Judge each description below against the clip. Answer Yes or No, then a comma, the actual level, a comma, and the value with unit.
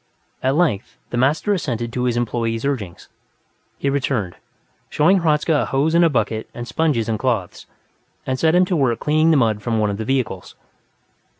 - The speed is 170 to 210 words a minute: Yes, average, 185 wpm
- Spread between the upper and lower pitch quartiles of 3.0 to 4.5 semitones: No, average, 5.1 semitones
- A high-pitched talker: No, low, 130 Hz